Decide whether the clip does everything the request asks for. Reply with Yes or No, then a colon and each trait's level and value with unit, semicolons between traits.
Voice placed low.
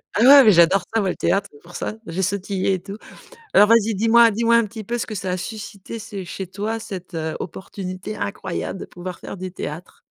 No: high, 200 Hz